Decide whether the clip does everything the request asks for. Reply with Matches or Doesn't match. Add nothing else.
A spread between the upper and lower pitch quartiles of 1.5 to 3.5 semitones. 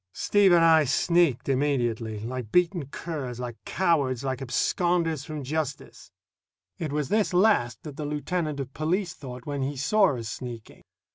Doesn't match